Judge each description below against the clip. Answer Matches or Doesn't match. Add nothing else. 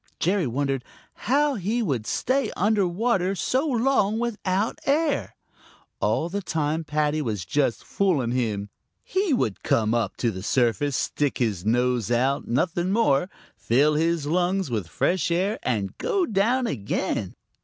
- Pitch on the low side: Doesn't match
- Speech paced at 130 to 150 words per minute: Matches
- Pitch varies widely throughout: Matches